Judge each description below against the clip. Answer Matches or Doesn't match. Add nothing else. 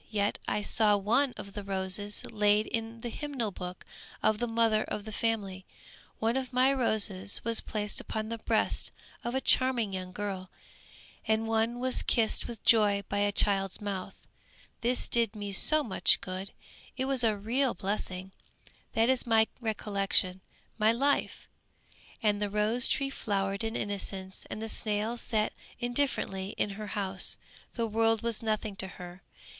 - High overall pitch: Matches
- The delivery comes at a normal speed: Matches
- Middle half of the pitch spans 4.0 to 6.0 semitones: Doesn't match